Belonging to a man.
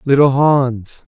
Yes: male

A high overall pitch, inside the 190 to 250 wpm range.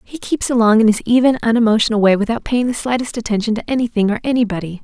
Yes: high, 225 Hz; average, 200 wpm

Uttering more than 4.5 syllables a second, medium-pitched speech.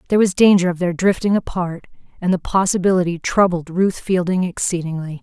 Yes: 5.8 syllables/s; medium, 180 Hz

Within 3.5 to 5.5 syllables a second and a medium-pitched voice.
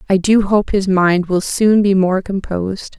No: 4.3 syllables/s; high, 195 Hz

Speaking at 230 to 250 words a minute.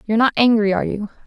Yes: fast, 235 wpm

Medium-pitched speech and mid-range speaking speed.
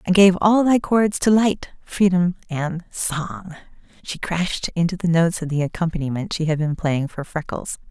Yes: medium, 175 Hz; average, 180 wpm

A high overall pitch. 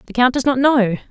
Yes: very high, 250 Hz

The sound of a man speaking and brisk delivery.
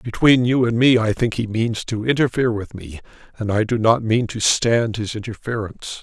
Yes: male; fast, 210 wpm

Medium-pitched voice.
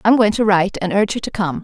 No: high, 200 Hz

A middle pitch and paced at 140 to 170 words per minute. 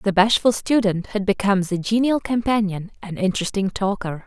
No: high, 200 Hz; average, 155 wpm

